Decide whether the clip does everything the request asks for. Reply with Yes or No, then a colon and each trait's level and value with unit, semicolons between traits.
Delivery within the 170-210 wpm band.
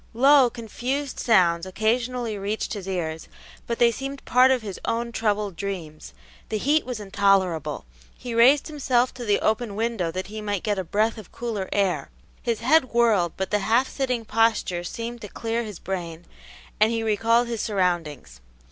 Yes: average, 175 wpm